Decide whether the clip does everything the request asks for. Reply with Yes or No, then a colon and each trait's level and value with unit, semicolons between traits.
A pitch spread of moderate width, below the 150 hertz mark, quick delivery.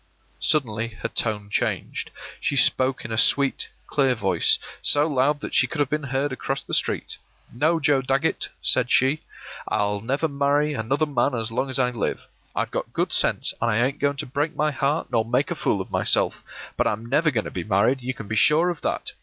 Yes: average, 4.2 semitones; low, 135 Hz; fast, 220 wpm